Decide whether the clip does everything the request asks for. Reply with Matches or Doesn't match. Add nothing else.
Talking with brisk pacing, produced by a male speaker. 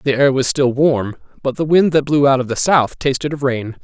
Matches